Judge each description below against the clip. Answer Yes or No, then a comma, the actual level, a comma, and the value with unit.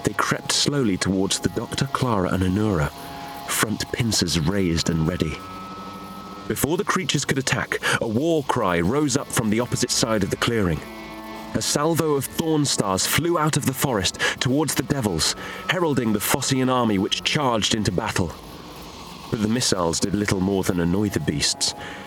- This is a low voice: Yes, low, 110 Hz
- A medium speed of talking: Yes, average, 170 wpm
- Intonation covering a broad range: Yes, wide, 6.1 semitones